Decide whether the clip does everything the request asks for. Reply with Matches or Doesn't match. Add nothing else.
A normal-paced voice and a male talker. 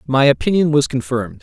Matches